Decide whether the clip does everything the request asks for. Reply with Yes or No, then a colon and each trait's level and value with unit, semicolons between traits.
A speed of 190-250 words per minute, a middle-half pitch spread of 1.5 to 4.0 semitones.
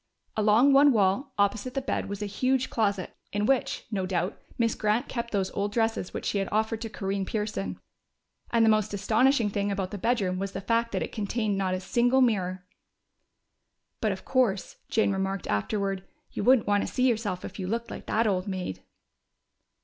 Yes: average, 195 wpm; average, 3.0 semitones